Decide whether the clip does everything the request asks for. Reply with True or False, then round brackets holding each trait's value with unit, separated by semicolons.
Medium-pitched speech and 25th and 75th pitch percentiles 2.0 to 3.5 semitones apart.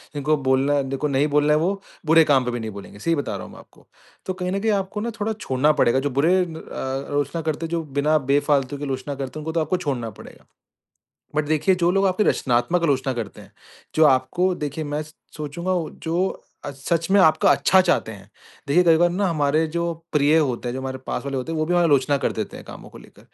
False (150 Hz; 4.2 semitones)